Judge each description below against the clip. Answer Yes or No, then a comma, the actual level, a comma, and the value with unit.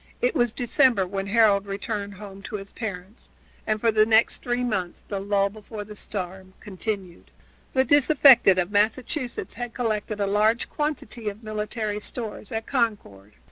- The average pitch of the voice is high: Yes, high, 215 Hz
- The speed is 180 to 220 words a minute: No, average, 160 wpm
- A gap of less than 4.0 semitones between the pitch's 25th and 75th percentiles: Yes, average, 2.8 semitones